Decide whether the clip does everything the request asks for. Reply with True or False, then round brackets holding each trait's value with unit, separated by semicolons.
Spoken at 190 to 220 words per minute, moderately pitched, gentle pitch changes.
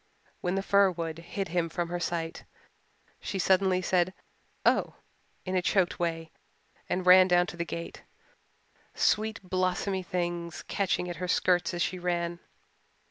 False (150 wpm; 180 Hz; 1.4 semitones)